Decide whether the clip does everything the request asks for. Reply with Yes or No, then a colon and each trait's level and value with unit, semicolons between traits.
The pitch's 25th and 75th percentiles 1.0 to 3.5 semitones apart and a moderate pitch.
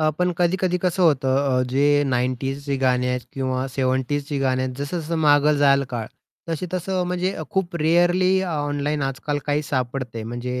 No: average, 4.6 semitones; medium, 145 Hz